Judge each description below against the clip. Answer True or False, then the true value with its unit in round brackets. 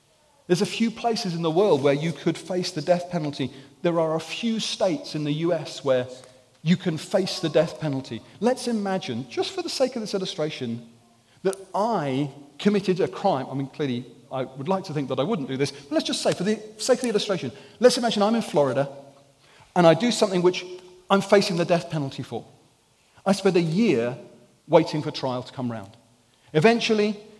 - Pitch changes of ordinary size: False (6.7 semitones)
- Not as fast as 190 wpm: False (205 wpm)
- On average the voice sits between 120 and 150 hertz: False (170 Hz)